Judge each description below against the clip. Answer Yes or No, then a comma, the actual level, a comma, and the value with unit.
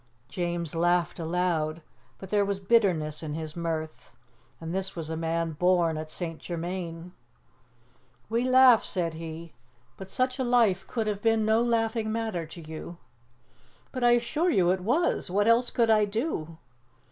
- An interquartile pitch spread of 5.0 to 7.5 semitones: Yes, wide, 5.4 semitones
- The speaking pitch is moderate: Yes, medium, 180 Hz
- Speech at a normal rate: Yes, average, 160 wpm